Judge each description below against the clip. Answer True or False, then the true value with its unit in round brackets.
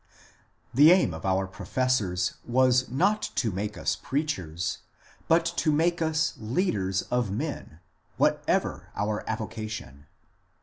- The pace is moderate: False (120 wpm)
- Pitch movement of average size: False (7.7 semitones)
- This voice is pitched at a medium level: False (115 Hz)